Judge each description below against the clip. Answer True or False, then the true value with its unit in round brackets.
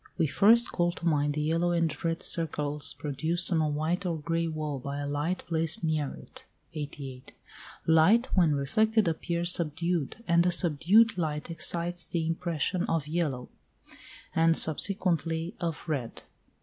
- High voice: False (165 Hz)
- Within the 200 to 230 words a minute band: False (150 wpm)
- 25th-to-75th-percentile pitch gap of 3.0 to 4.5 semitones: False (2.5 semitones)